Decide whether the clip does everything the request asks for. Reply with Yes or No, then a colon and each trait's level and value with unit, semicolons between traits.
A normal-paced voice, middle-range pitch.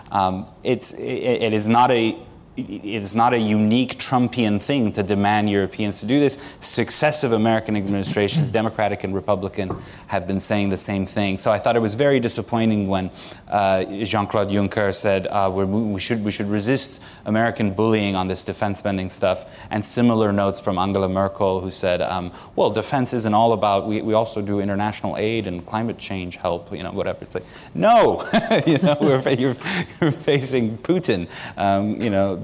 No: average, 180 wpm; low, 105 Hz